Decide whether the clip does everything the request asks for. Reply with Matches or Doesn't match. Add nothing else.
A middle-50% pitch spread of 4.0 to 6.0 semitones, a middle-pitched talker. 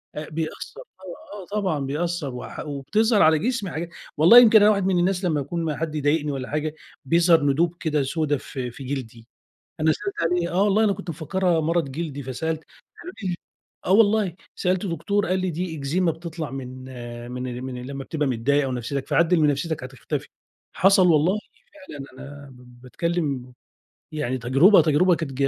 Matches